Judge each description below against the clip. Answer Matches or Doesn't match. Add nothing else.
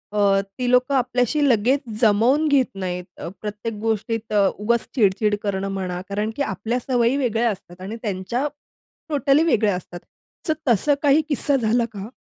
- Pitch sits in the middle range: Doesn't match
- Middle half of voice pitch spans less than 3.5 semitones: Doesn't match